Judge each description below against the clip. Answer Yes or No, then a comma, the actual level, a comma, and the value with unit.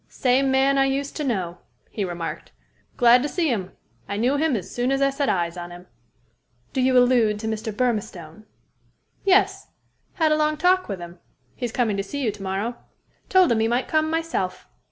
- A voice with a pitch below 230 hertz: No, high, 245 Hz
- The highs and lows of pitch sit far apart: Yes, wide, 5.8 semitones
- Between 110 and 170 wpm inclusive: No, average, 195 wpm